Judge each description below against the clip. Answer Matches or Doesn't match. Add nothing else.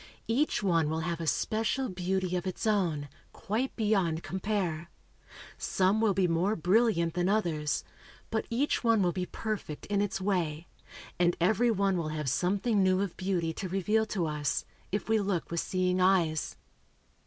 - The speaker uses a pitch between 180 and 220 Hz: Matches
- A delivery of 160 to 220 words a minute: Matches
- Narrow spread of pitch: Doesn't match